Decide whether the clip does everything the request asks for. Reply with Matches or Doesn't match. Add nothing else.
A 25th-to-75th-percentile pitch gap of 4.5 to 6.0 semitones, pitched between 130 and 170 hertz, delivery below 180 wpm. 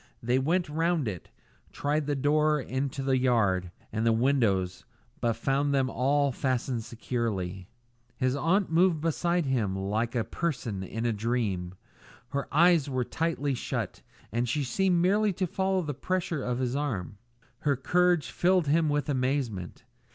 Matches